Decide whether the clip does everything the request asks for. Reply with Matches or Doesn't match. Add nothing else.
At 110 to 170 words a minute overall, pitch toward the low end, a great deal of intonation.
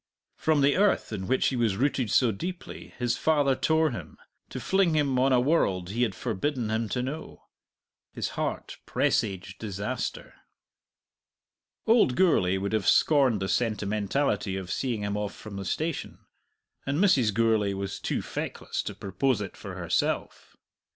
Matches